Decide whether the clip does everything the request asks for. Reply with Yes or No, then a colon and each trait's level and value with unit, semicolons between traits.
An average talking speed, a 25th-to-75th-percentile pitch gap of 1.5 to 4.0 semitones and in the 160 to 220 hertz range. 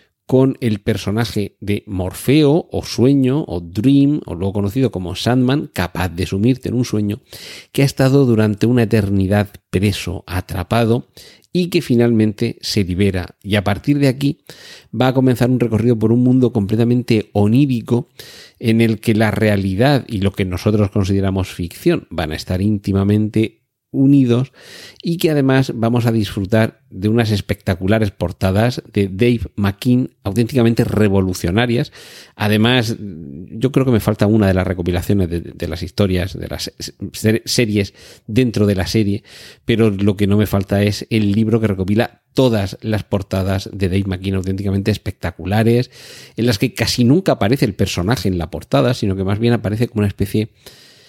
No: average, 165 wpm; average, 3.6 semitones; low, 110 Hz